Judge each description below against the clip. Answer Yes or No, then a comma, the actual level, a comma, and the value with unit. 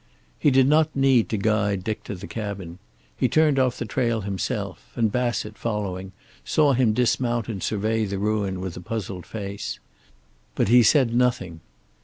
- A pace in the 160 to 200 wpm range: Yes, average, 170 wpm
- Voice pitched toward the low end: Yes, low, 110 Hz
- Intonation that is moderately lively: Yes, average, 3.9 semitones